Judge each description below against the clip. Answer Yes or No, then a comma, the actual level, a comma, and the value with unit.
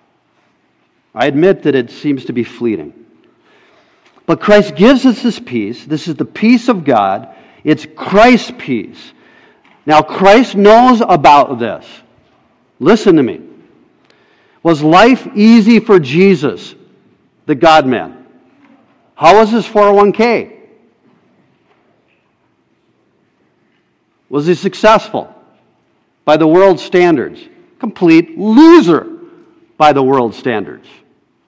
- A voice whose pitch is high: Yes, high, 210 Hz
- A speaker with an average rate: No, slow, 105 wpm